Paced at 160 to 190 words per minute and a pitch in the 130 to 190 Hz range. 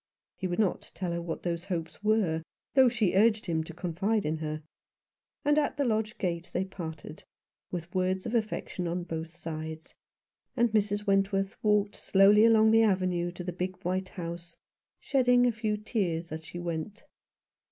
Yes: average, 175 wpm; medium, 185 Hz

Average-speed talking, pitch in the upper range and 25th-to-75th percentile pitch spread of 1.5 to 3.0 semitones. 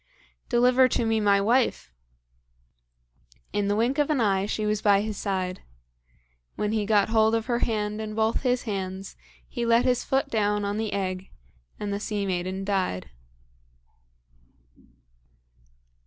Yes: average, 150 wpm; high, 210 Hz; narrow, 2.5 semitones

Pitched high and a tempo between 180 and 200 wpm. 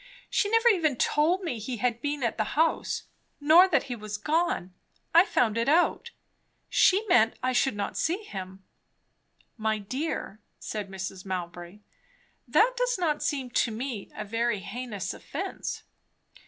No: high, 245 Hz; average, 155 wpm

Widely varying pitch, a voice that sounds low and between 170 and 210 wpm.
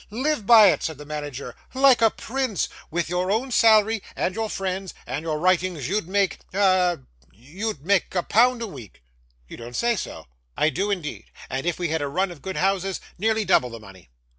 No: wide, 5.9 semitones; medium, 185 Hz; average, 200 wpm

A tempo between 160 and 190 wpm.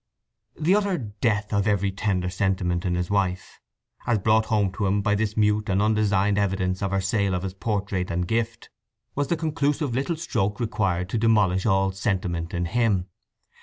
Yes: average, 180 wpm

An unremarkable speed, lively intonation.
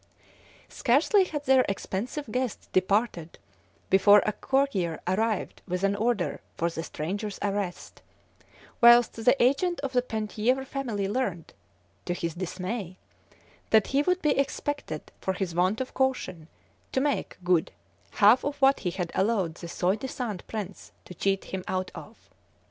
Yes: average, 150 wpm; wide, 5.9 semitones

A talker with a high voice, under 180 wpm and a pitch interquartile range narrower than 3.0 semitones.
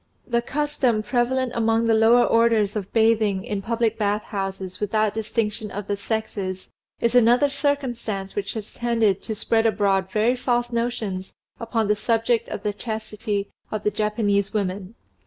Yes: high, 220 Hz; average, 155 wpm; narrow, 2.5 semitones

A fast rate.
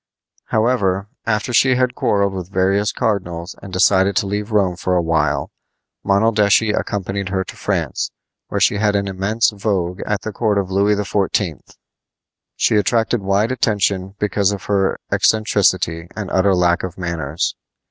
No: average, 155 wpm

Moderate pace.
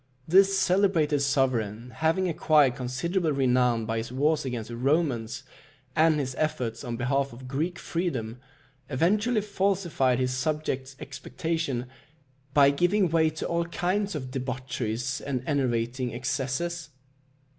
No: slow, 125 wpm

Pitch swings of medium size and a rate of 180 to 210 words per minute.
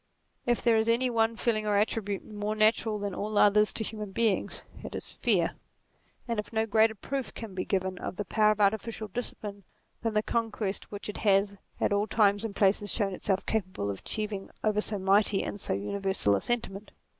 No: narrow, 1.9 semitones; average, 195 wpm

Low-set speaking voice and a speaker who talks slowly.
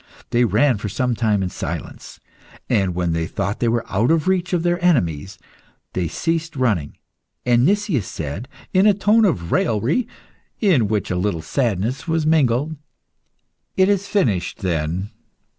No: low, 120 Hz; average, 160 wpm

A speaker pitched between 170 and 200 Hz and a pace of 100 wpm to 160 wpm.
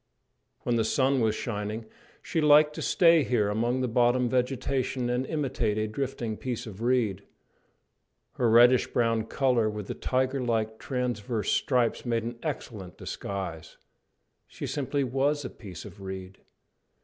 No: low, 120 Hz; average, 150 wpm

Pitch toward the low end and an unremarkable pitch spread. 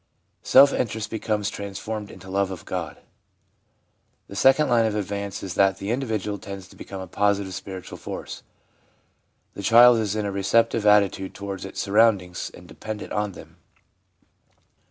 No: low, 100 Hz; narrow, 2.2 semitones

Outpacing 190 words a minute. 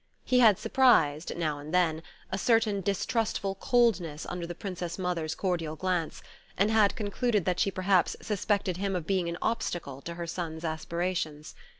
No: average, 165 wpm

